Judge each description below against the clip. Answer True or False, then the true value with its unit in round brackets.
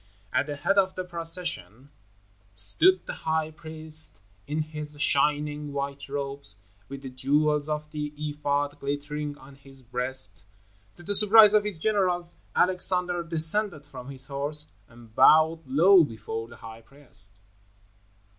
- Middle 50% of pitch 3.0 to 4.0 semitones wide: True (3.3 semitones)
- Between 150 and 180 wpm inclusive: False (140 wpm)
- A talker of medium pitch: True (150 Hz)